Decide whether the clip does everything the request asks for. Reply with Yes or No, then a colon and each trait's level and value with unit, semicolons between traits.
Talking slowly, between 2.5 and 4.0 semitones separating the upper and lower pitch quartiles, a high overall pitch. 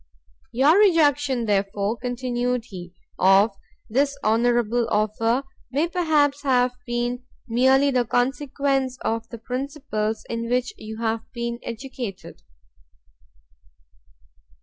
Yes: slow, 105 wpm; average, 3.2 semitones; high, 245 Hz